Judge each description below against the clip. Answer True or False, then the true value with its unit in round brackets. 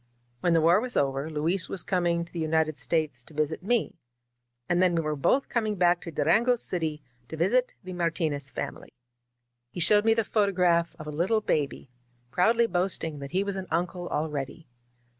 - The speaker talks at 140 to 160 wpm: False (185 wpm)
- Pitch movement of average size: True (3.6 semitones)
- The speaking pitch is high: False (170 Hz)